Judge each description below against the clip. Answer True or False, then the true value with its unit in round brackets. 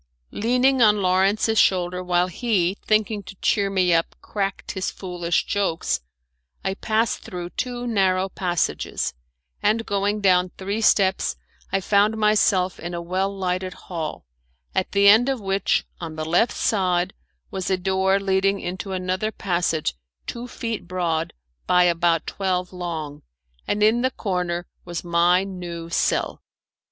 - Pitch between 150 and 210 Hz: True (190 Hz)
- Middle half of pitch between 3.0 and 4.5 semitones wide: False (2.5 semitones)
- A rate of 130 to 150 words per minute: True (145 wpm)